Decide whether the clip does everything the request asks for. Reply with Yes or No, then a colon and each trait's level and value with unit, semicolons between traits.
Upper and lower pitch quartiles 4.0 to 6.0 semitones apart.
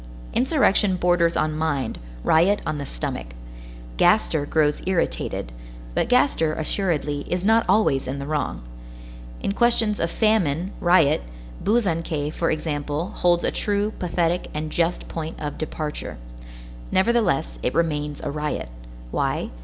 Yes: average, 4.3 semitones